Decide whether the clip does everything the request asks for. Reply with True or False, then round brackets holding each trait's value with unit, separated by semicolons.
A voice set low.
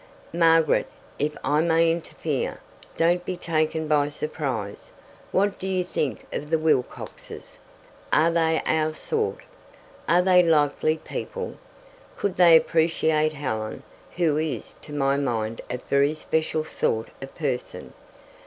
False (155 Hz)